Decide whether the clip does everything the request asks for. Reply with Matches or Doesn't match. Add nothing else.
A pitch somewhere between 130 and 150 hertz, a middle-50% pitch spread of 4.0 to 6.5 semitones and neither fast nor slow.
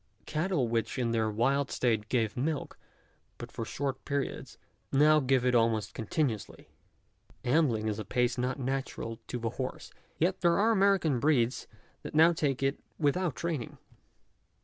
Matches